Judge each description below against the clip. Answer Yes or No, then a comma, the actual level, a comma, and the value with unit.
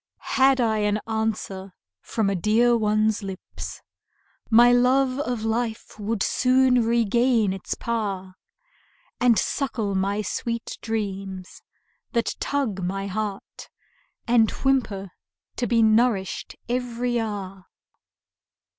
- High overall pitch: Yes, high, 220 Hz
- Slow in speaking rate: Yes, slow, 110 wpm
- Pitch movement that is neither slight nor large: Yes, average, 3.4 semitones